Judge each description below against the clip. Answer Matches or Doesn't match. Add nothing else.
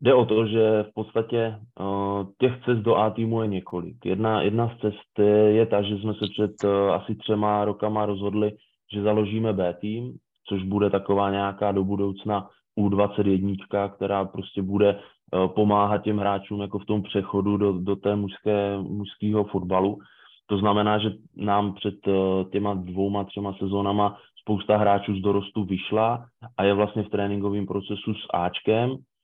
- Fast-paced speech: Doesn't match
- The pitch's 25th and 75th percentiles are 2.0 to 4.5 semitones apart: Doesn't match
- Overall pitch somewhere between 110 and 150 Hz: Doesn't match